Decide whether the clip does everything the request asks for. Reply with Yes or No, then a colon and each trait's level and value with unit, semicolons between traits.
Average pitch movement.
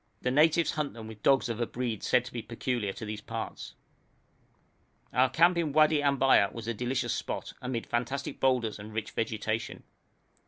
Yes: average, 3.5 semitones